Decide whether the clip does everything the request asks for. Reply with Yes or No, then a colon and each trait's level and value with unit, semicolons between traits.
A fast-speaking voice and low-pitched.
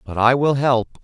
Yes: fast, 230 wpm; low, 125 Hz